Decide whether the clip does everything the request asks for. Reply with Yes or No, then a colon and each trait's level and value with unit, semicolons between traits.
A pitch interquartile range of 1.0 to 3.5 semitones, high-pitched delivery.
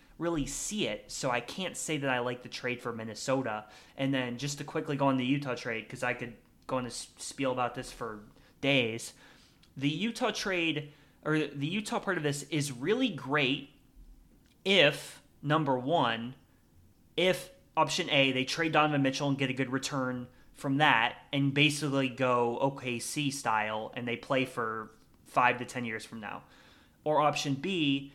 No: average, 3.2 semitones; low, 135 Hz